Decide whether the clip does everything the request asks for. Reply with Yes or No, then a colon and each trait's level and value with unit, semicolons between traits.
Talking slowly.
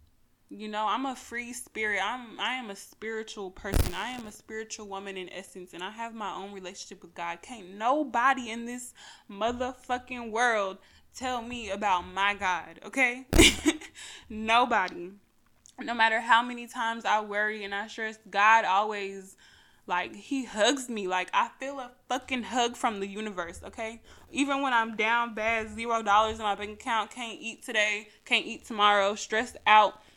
No: average, 170 wpm